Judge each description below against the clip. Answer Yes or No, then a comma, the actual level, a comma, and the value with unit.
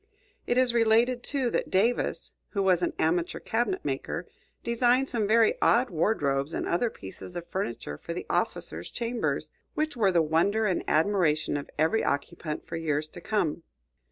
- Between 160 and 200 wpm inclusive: Yes, average, 165 wpm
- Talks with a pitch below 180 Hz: No, high, 190 Hz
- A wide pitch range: Yes, wide, 6.7 semitones